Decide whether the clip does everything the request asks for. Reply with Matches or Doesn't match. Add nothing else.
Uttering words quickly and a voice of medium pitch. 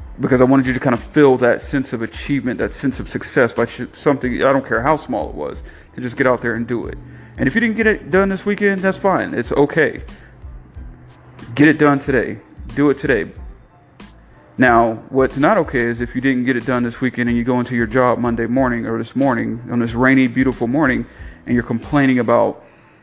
Doesn't match